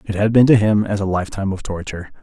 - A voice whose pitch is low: Yes, low, 100 Hz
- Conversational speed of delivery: No, fast, 270 wpm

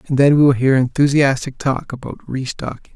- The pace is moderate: Yes, average, 180 wpm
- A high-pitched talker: No, low, 135 Hz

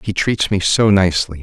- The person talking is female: No, male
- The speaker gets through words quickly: Yes, fast, 210 wpm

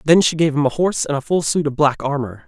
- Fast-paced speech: Yes, fast, 315 wpm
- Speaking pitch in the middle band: Yes, medium, 145 Hz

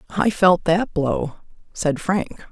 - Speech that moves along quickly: No, average, 145 wpm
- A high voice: No, medium, 175 Hz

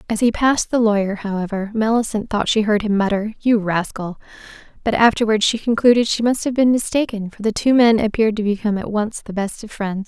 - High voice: Yes, high, 215 Hz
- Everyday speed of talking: No, fast, 215 wpm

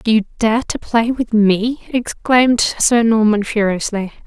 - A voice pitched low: No, high, 225 Hz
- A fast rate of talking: No, average, 155 wpm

